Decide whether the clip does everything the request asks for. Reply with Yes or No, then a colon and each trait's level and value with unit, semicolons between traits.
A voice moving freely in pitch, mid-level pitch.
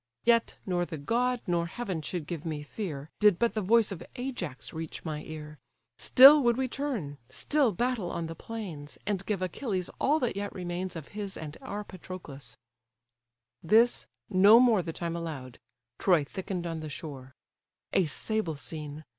Yes: wide, 6.0 semitones; medium, 180 Hz